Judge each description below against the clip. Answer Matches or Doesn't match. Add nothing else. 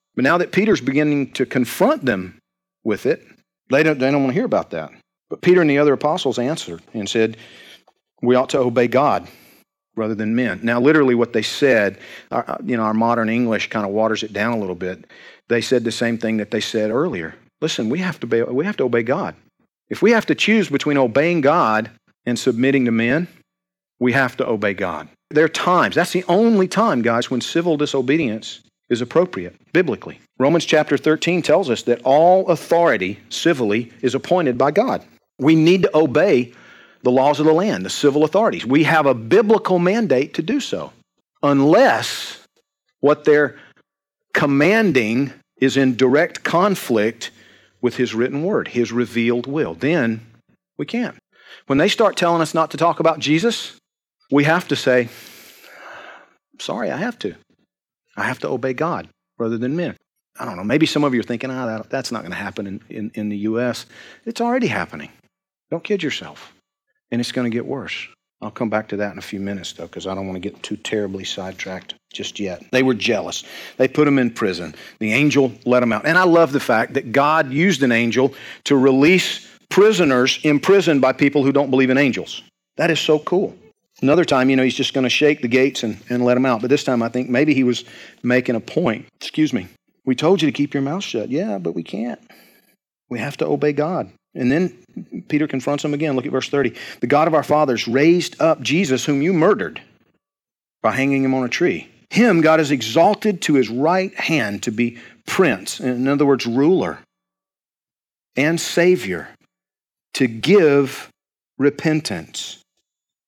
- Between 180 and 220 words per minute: Matches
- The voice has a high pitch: Doesn't match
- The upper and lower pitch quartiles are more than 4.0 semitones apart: Matches